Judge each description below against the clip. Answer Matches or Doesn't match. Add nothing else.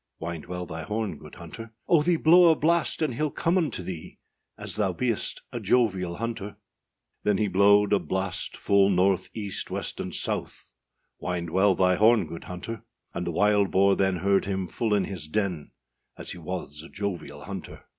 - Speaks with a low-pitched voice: Matches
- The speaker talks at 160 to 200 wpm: Matches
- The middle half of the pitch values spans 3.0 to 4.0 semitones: Matches